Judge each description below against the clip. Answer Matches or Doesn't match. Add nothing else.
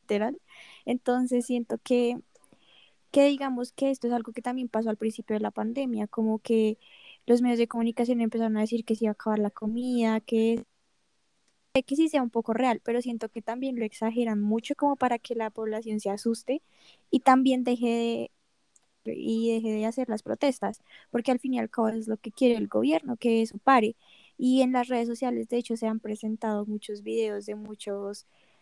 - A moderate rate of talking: Doesn't match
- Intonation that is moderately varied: Doesn't match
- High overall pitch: Matches